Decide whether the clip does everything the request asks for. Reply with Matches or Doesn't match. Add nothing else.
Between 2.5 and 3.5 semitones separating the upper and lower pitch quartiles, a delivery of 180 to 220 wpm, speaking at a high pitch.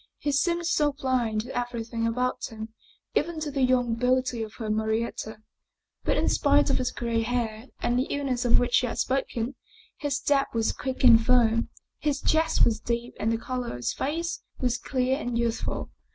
Matches